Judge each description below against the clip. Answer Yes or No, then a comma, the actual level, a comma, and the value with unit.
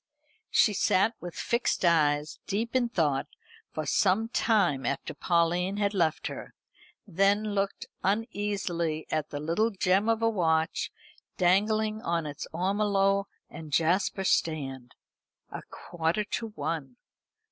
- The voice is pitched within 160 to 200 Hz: Yes, medium, 185 Hz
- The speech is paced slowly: Yes, slow, 125 wpm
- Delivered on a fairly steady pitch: No, average, 4.5 semitones